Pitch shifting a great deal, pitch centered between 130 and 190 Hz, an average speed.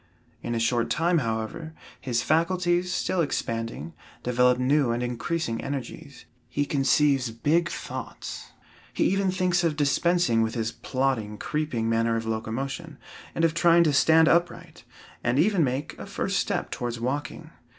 Yes: wide, 6.0 semitones; medium, 140 Hz; average, 150 wpm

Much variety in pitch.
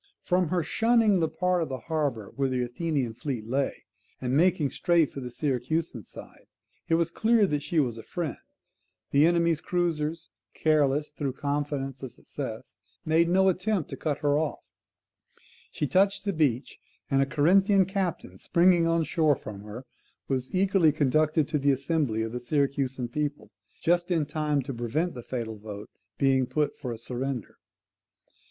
No: average, 4.3 semitones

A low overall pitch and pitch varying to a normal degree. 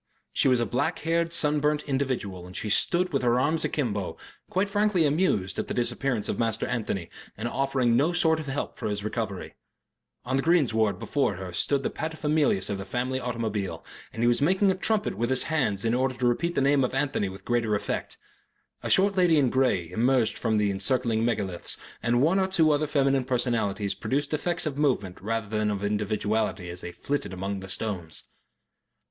No: low, 125 Hz; wide, 5.9 semitones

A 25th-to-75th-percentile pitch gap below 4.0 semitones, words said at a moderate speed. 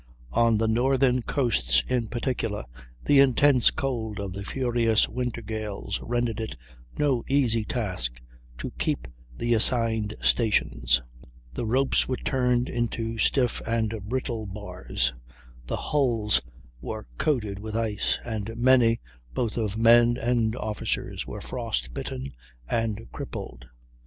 No: average, 2.8 semitones; slow, 125 wpm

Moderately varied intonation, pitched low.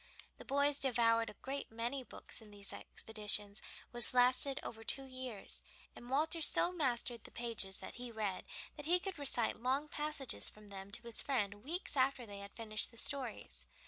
No: average, 4.3 semitones; high, 240 Hz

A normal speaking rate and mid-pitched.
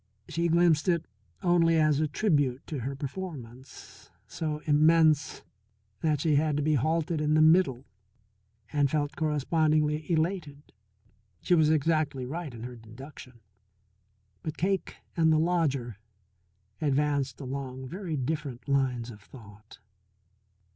No: slow, 125 wpm; medium, 150 Hz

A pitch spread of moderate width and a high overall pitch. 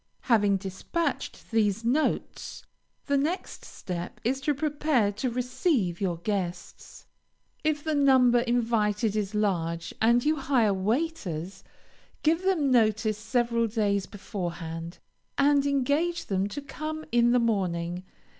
No: wide, 6.2 semitones; high, 230 Hz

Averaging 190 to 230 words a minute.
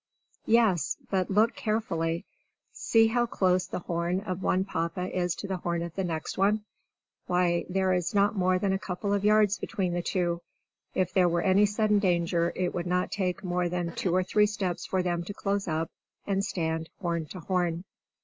Yes: average, 195 wpm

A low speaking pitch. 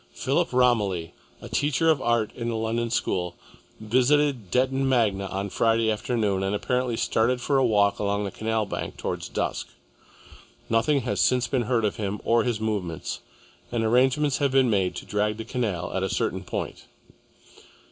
Yes: low, 115 Hz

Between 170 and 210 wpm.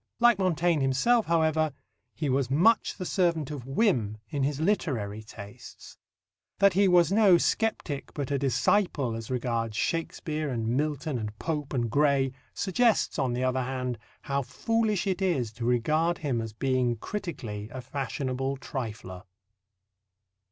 No: average, 145 wpm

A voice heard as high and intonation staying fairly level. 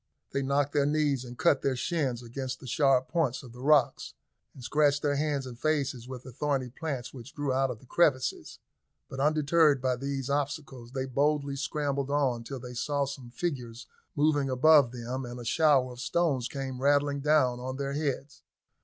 No: low, 135 Hz; narrow, 2.3 semitones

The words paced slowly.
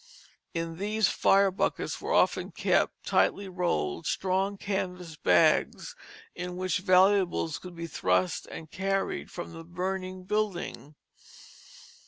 Yes: slow, 120 wpm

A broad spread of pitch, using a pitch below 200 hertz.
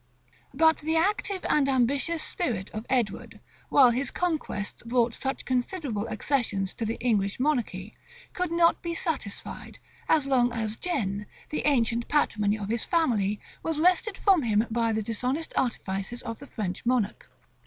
No: wide, 6.0 semitones; high, 245 Hz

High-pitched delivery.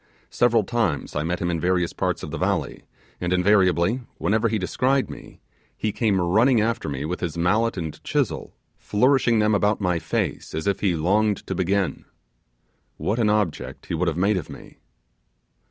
No: low, 100 Hz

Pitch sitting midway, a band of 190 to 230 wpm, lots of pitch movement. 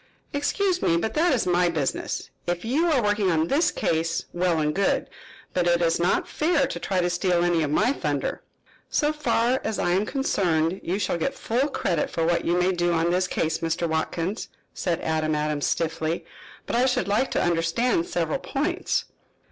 Yes: medium, 175 Hz; average, 195 wpm; wide, 6.6 semitones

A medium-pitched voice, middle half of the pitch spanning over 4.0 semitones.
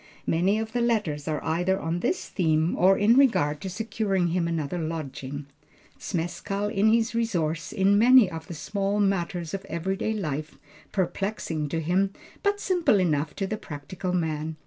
Yes: medium, 180 Hz; average, 4.4 semitones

